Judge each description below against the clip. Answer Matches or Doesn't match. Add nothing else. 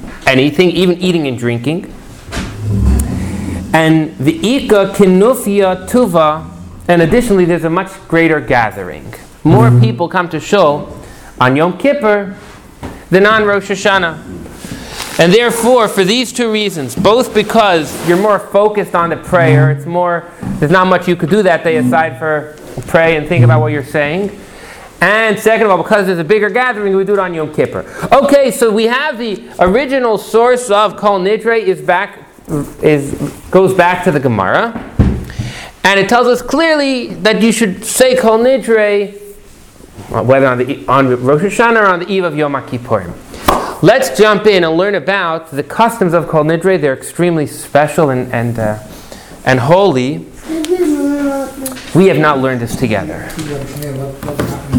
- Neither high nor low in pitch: Matches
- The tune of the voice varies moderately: Doesn't match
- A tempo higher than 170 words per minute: Doesn't match